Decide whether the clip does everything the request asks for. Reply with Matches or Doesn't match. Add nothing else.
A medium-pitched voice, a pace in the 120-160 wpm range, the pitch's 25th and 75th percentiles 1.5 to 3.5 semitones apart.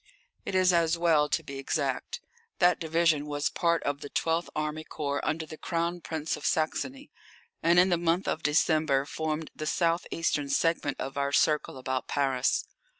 Doesn't match